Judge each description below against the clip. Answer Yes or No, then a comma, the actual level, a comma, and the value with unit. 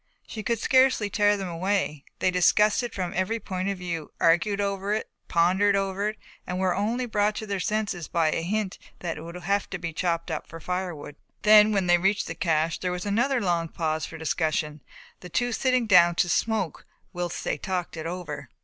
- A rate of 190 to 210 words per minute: Yes, fast, 205 wpm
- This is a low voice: No, medium, 185 Hz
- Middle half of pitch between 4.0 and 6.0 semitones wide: No, average, 3.5 semitones